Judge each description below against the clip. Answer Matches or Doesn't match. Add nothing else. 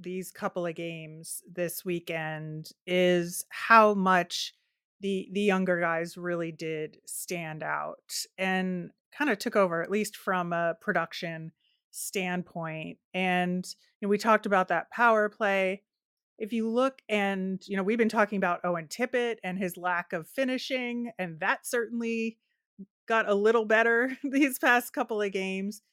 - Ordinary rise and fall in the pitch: Matches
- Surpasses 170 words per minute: Doesn't match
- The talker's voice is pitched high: Matches